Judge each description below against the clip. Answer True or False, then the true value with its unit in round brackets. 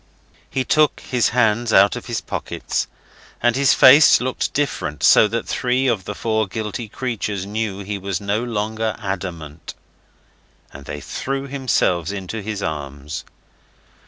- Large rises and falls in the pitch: False (4.2 semitones)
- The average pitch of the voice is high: False (110 Hz)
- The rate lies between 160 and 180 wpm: False (145 wpm)